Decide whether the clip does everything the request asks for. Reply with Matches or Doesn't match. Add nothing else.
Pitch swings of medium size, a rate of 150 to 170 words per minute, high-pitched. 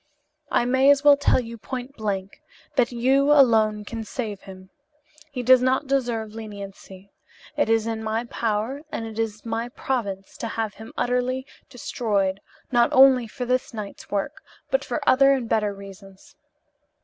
Matches